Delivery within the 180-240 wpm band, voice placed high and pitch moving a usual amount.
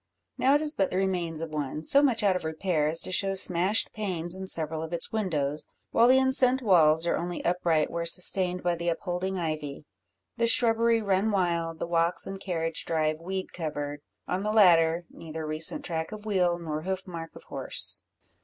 No: average, 195 wpm; medium, 175 Hz; average, 3.1 semitones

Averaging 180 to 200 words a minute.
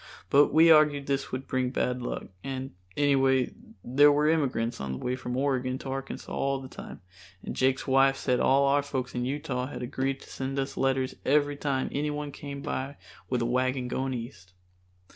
Yes: average, 190 wpm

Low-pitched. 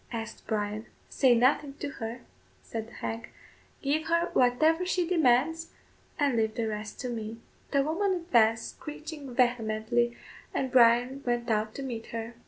No: high, 245 Hz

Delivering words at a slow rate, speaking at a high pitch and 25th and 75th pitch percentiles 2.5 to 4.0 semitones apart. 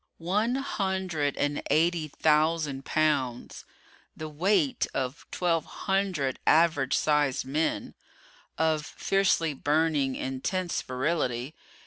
No: slow, 95 wpm; medium, 155 Hz; average, 3.6 semitones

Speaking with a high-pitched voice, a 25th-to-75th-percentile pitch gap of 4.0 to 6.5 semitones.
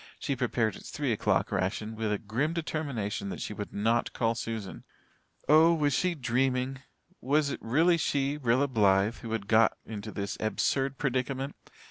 No: low, 120 Hz; average, 4.5 semitones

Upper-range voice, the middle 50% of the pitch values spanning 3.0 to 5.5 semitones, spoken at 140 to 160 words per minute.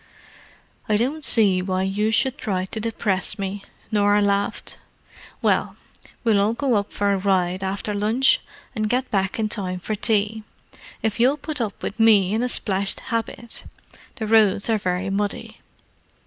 No: high, 210 Hz; narrow, 2.5 semitones; average, 155 wpm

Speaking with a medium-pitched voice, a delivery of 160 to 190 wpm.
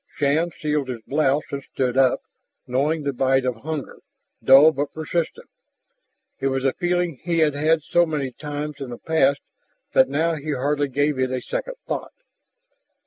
Yes: medium, 145 Hz; average, 170 wpm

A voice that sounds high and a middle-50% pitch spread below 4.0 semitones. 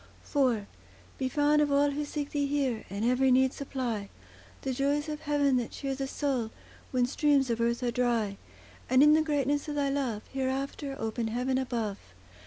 Yes: very high, 265 Hz; average, 3.0 semitones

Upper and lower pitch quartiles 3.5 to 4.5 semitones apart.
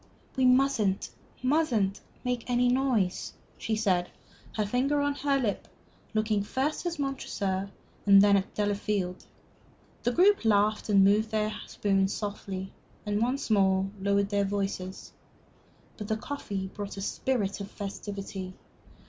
Yes: average, 4.0 semitones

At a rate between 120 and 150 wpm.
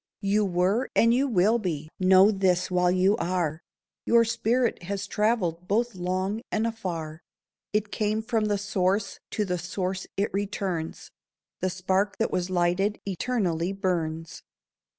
Yes: average, 145 wpm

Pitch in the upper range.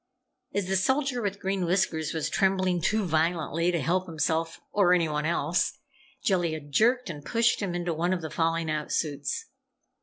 No: medium, 175 Hz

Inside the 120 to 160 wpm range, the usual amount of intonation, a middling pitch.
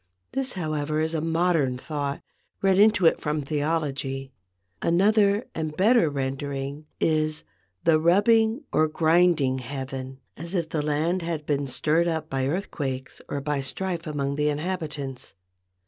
Yes: average, 140 wpm; average, 3.4 semitones; medium, 155 Hz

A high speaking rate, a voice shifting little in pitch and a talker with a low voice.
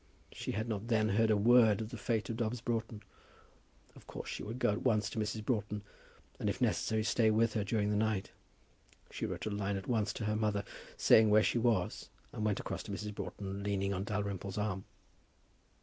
Yes: fast, 210 wpm; narrow, 1.6 semitones; low, 105 Hz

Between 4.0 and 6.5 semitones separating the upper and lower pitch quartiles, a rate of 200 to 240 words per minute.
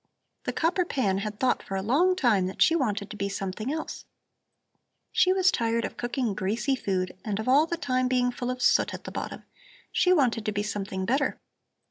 Yes: average, 5.2 semitones; fast, 205 wpm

